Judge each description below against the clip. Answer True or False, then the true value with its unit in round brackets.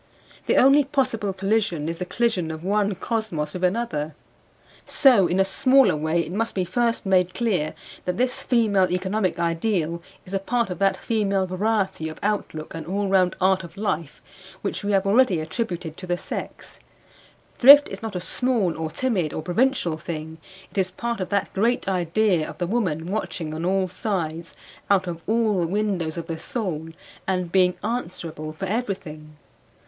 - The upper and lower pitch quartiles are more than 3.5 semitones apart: True (4.4 semitones)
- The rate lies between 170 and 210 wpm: True (175 wpm)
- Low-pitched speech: False (190 Hz)